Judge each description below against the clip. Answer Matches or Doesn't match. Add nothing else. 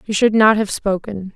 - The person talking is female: Matches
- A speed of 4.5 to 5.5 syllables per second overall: Matches